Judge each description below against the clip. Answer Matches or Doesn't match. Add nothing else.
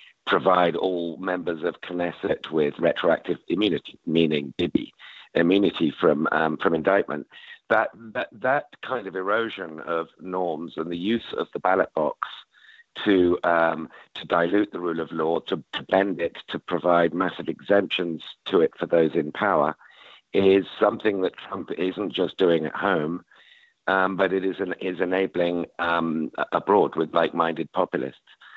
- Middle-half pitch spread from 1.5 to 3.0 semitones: Matches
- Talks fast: Doesn't match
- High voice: Doesn't match